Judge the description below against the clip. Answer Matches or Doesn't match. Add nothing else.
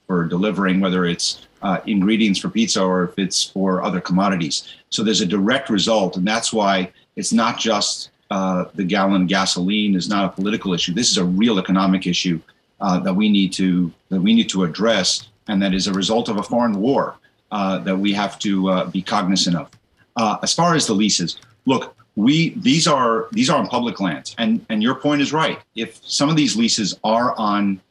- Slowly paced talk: Doesn't match